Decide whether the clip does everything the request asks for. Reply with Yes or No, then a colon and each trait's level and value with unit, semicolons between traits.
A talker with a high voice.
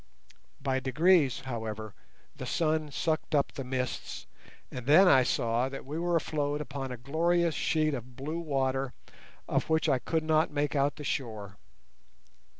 No: medium, 140 Hz